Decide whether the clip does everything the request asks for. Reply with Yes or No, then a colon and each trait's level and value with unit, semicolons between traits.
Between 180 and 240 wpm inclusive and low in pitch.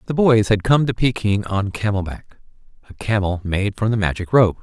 Yes: fast, 205 wpm; low, 105 Hz